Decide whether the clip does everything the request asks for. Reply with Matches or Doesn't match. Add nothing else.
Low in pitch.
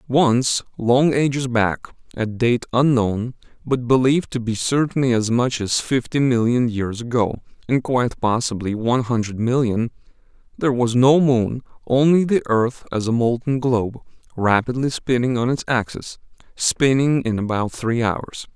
Matches